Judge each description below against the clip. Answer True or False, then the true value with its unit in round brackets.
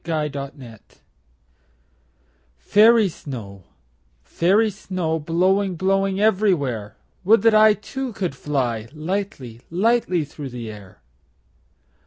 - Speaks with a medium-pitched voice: True (170 Hz)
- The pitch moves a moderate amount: False (7.5 semitones)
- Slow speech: True (100 wpm)